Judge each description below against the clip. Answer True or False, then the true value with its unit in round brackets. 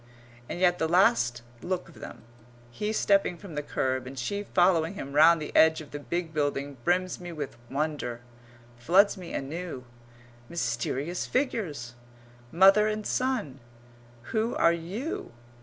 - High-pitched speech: False (170 Hz)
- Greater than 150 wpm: False (145 wpm)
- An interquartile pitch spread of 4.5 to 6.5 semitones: True (5.1 semitones)